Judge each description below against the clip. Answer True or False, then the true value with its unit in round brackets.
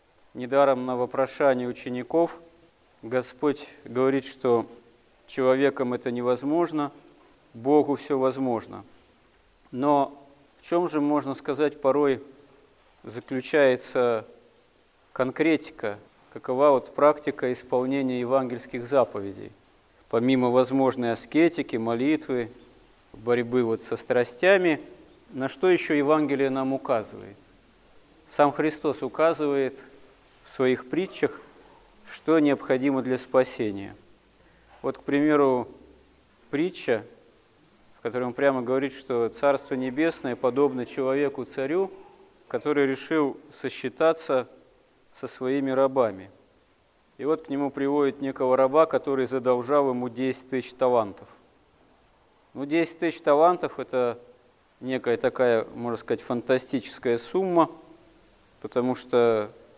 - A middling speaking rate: False (100 wpm)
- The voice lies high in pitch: False (135 Hz)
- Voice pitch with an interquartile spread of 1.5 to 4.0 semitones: True (2.7 semitones)